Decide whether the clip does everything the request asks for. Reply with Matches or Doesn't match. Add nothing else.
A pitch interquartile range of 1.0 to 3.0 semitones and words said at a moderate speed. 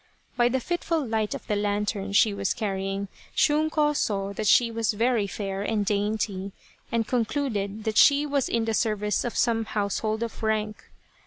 Matches